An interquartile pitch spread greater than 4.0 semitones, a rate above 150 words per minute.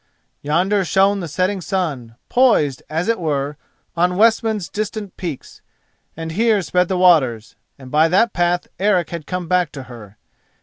Yes: average, 4.6 semitones; average, 160 wpm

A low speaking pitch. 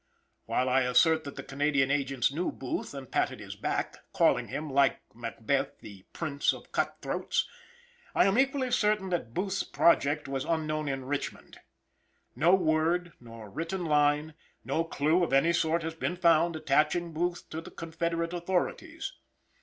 No: medium, 155 Hz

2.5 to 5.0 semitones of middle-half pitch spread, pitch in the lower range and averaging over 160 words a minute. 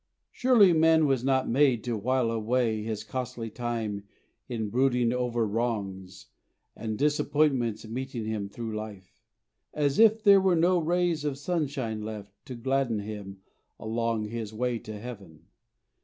No: average, 4.2 semitones; low, 120 Hz; average, 140 wpm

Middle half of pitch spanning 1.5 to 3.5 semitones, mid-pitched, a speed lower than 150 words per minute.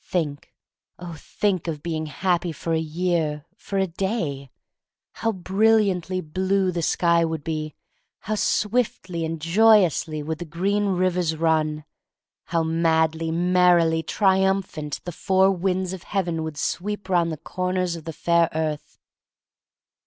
Yes: average, 2.9 semitones; medium, 170 Hz; average, 140 wpm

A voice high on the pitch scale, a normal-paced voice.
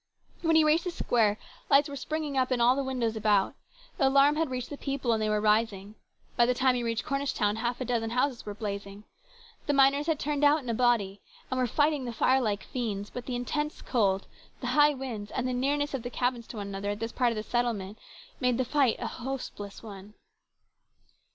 No: high, 245 Hz; fast, 230 wpm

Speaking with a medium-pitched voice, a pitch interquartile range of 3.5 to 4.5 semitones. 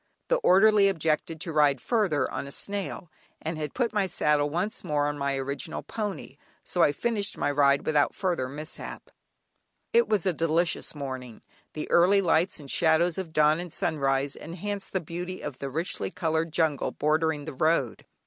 Yes: medium, 160 Hz; average, 4.0 semitones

